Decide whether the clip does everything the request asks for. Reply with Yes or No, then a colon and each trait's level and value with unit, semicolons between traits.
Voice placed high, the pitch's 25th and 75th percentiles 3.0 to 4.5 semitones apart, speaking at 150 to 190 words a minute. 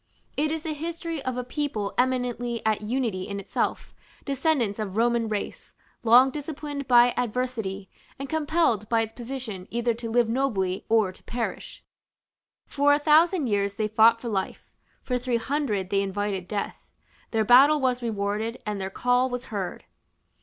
Yes: high, 235 Hz; average, 4.2 semitones; average, 160 wpm